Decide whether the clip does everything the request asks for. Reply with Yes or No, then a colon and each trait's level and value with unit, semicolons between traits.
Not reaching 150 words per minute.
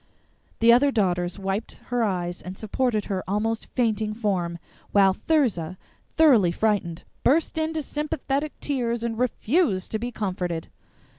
Yes: slow, 135 wpm